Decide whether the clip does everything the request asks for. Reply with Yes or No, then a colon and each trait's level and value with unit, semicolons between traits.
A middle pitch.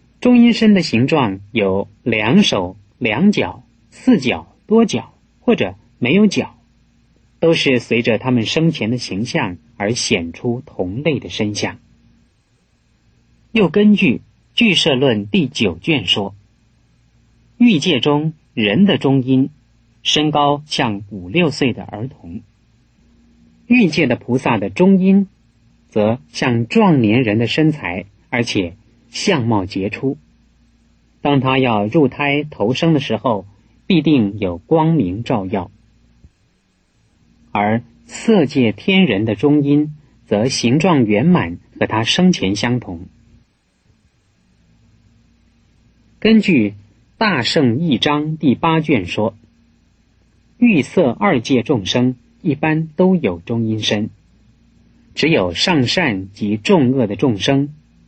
No: low, 125 Hz